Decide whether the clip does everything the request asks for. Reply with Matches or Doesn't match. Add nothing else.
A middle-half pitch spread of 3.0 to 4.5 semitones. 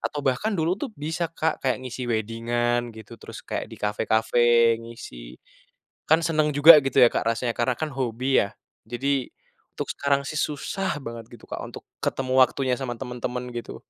Matches